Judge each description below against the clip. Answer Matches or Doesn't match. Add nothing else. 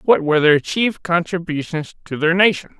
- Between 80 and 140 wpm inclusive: Doesn't match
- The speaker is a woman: Doesn't match